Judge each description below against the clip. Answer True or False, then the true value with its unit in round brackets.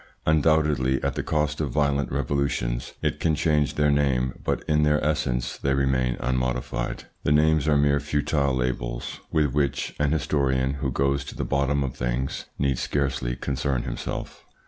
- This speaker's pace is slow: False (165 wpm)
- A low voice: True (70 Hz)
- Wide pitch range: False (2.4 semitones)